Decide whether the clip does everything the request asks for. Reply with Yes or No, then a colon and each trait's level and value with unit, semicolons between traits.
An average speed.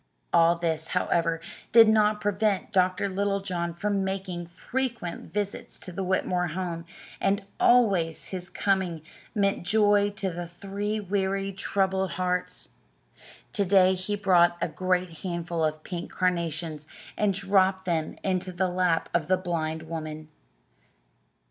No: slow, 130 wpm